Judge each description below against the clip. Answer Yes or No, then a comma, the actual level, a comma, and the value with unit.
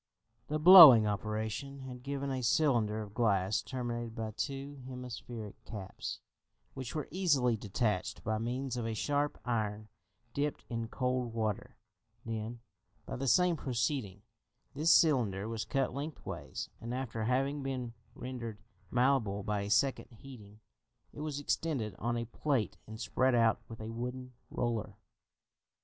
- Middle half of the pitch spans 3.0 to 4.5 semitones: Yes, average, 3.8 semitones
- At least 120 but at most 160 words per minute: Yes, average, 140 wpm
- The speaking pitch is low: Yes, low, 120 Hz